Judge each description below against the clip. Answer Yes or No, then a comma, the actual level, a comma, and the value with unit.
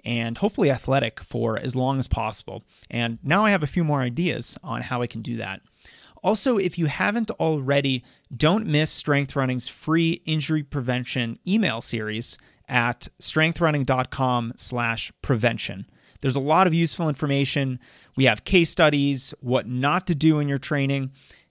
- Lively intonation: No, average, 4.3 semitones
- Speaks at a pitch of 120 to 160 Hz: Yes, medium, 140 Hz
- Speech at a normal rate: Yes, average, 155 wpm